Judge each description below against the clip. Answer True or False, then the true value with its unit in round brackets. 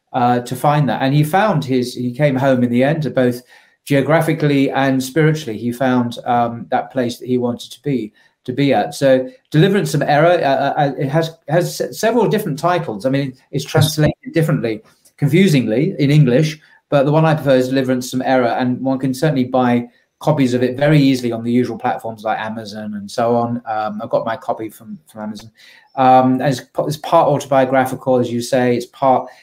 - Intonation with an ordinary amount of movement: True (3.3 semitones)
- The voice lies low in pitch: True (130 Hz)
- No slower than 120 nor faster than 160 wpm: False (200 wpm)